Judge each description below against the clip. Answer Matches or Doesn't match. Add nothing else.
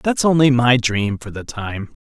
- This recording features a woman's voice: Doesn't match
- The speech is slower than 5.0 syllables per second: Matches